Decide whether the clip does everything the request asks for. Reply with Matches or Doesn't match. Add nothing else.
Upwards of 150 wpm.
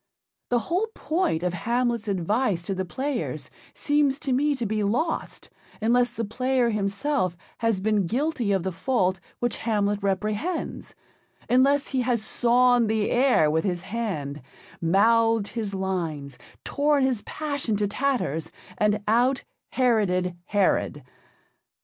Doesn't match